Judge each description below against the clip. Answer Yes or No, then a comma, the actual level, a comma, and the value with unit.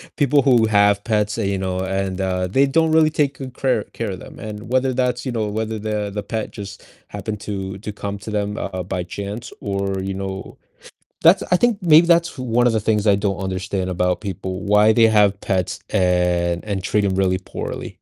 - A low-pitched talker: Yes, low, 105 Hz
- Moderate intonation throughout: Yes, average, 3.8 semitones